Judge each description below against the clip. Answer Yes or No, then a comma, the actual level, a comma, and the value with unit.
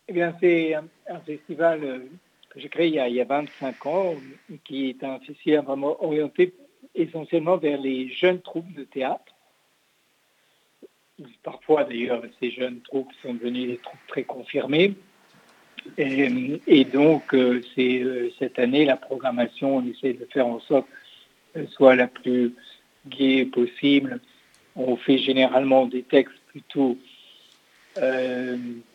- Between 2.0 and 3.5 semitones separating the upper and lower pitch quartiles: No, average, 4.4 semitones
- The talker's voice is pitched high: No, low, 135 Hz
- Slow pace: Yes, slow, 135 wpm